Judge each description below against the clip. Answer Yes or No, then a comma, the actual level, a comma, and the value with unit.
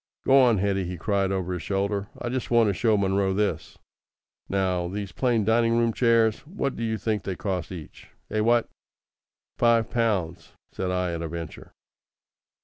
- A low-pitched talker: Yes, low, 100 Hz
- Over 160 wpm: Yes, average, 170 wpm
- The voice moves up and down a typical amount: Yes, average, 3.9 semitones